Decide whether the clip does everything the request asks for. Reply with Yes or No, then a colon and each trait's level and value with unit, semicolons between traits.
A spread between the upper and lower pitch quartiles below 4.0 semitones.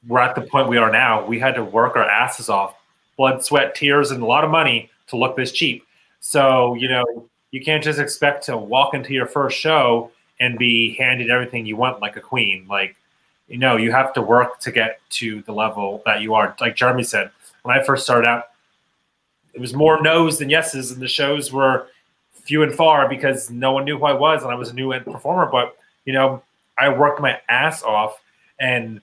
Yes: average, 2.9 semitones